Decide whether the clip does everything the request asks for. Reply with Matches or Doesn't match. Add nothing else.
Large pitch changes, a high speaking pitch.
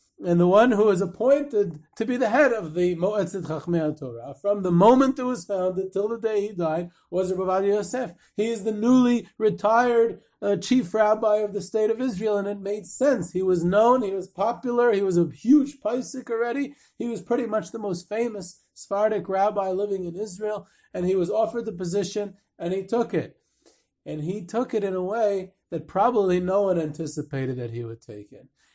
Doesn't match